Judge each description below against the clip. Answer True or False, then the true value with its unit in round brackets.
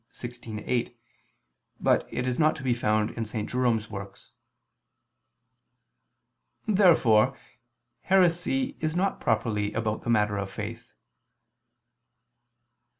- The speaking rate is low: True (110 wpm)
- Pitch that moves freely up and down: True (6.1 semitones)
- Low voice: True (120 Hz)